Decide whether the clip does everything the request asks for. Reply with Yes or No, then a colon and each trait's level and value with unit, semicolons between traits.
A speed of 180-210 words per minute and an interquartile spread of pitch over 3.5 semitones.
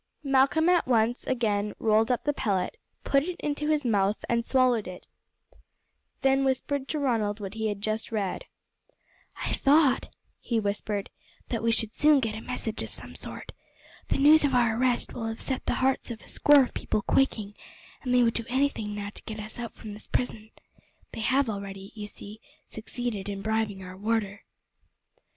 Yes: average, 185 wpm; average, 4.0 semitones